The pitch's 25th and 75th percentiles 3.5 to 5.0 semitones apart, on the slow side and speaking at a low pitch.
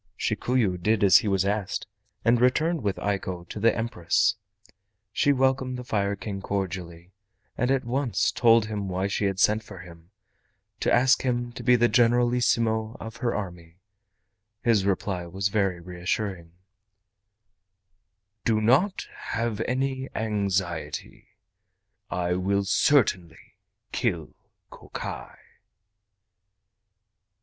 Yes: average, 4.3 semitones; slow, 120 wpm; low, 105 Hz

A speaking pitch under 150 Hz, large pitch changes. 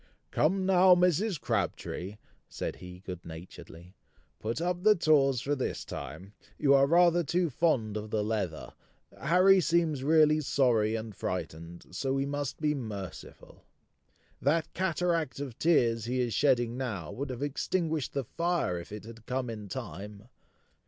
Yes: low, 135 Hz; wide, 7.2 semitones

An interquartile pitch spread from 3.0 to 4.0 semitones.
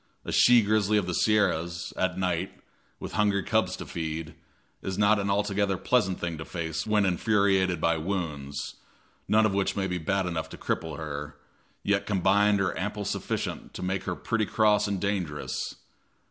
Yes: average, 3.3 semitones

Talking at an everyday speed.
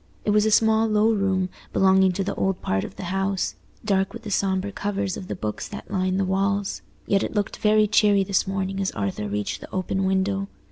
No: fast, 215 wpm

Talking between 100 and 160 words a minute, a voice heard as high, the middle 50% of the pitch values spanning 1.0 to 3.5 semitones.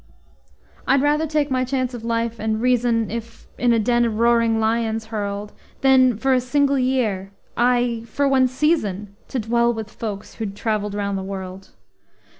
No: average, 170 wpm; high, 230 Hz; average, 3.1 semitones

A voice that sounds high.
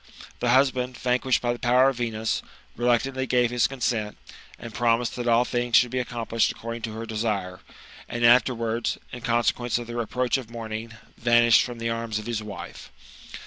No: low, 120 Hz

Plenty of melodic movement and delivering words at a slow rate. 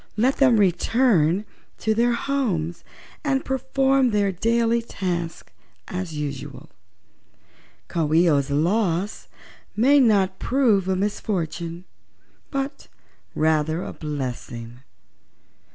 Yes: wide, 6.4 semitones; slow, 100 wpm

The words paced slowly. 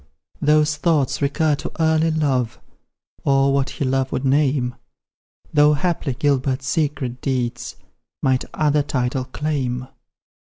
Yes: slow, 120 wpm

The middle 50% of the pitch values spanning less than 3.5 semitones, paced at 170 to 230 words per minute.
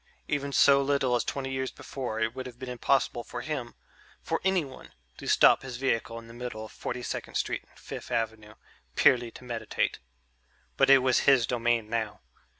Yes: narrow, 2.6 semitones; average, 185 wpm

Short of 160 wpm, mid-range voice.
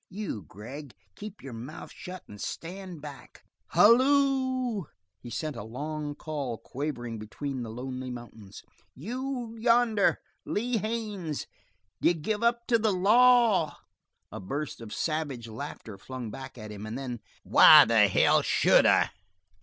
Yes: average, 140 wpm; medium, 155 Hz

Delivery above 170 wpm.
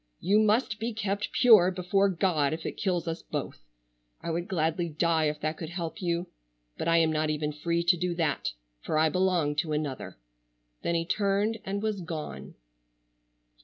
Yes: average, 180 wpm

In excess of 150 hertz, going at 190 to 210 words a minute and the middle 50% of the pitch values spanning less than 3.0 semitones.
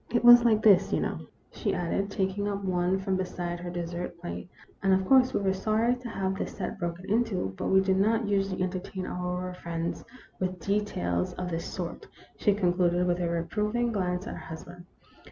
Yes: high, 190 Hz; average, 200 wpm; narrow, 2.5 semitones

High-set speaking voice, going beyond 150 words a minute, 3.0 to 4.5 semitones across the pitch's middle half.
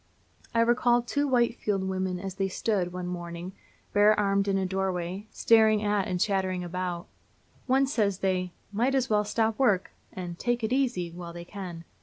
Yes: high, 195 Hz; average, 180 wpm; average, 3.6 semitones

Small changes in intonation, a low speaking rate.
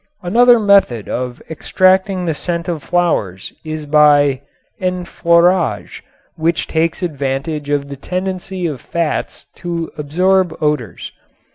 No: average, 3.9 semitones; slow, 115 wpm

